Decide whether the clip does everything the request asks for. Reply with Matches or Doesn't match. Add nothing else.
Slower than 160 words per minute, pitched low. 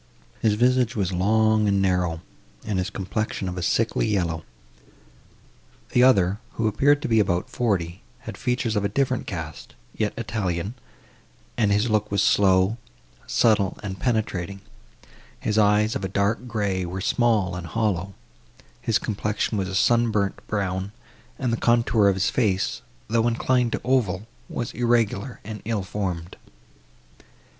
Matches